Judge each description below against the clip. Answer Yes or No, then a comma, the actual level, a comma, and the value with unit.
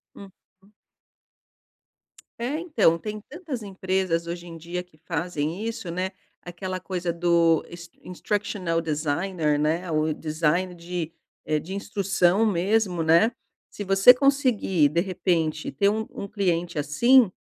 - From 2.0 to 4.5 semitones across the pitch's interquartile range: Yes, average, 3.4 semitones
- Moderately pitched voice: Yes, medium, 180 Hz